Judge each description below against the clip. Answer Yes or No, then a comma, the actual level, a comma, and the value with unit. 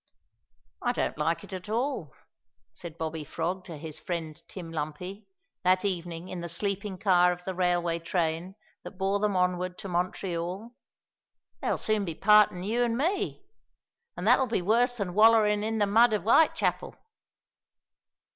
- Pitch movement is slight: No, average, 3.7 semitones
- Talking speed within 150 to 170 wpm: Yes, average, 155 wpm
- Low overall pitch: No, medium, 185 Hz